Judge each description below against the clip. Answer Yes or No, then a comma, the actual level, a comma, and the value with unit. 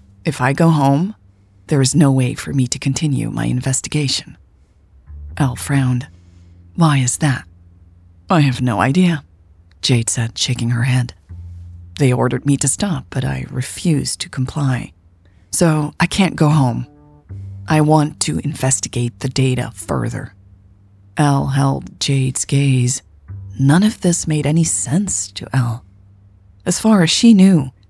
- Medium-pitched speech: No, low, 130 Hz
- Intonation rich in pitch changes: Yes, wide, 6.9 semitones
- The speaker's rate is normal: Yes, average, 145 wpm